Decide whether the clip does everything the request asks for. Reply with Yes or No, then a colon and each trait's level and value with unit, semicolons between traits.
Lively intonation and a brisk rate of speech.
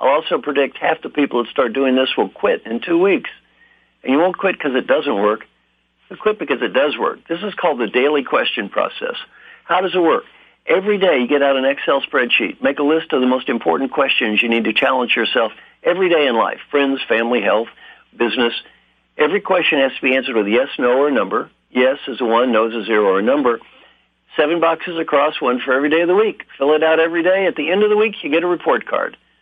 Yes: wide, 5.7 semitones; fast, 240 wpm